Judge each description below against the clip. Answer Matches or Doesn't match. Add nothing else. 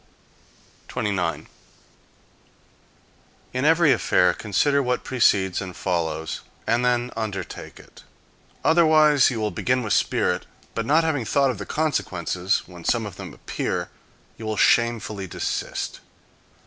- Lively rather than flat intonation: Matches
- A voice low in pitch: Matches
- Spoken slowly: Matches